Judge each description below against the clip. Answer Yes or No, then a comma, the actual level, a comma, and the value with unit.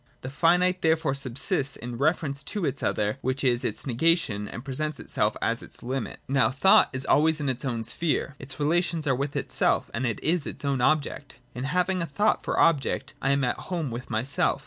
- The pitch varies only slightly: No, average, 4.0 semitones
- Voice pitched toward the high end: No, medium, 140 Hz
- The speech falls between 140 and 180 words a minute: No, fast, 205 wpm